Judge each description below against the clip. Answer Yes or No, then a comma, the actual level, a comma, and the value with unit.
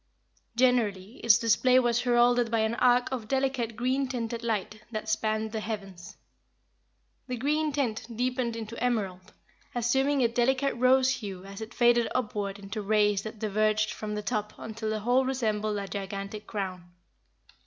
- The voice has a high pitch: Yes, high, 225 Hz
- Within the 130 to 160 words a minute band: Yes, average, 155 wpm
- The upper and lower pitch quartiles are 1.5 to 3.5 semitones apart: Yes, average, 2.9 semitones